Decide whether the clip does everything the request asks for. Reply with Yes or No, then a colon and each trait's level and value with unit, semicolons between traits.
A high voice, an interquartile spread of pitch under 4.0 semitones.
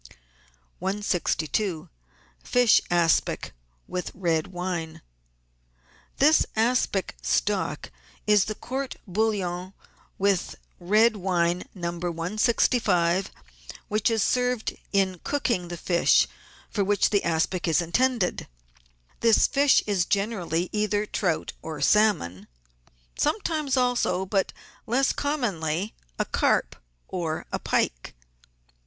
No: high, 195 Hz; average, 4.5 semitones